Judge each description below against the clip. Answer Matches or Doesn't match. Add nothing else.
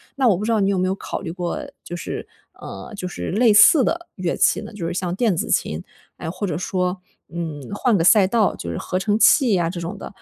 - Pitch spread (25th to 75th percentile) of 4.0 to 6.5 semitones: Doesn't match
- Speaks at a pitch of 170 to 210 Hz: Matches